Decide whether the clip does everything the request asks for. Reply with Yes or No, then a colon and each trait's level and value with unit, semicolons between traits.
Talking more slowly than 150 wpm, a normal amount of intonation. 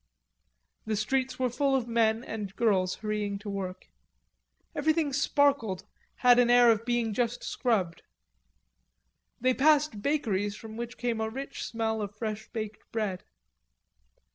Yes: average, 140 wpm; average, 3.1 semitones